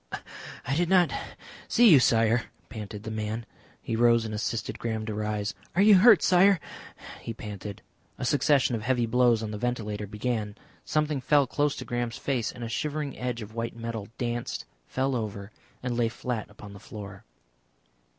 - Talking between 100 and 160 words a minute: No, average, 175 wpm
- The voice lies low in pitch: Yes, low, 115 Hz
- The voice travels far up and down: No, average, 3.5 semitones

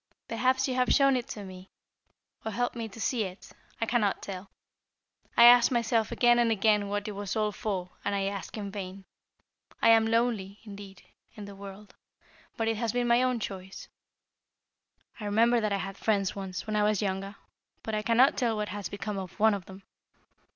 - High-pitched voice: Yes, high, 210 Hz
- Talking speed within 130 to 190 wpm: No, average, 200 wpm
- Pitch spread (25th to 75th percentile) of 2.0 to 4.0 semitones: Yes, average, 2.7 semitones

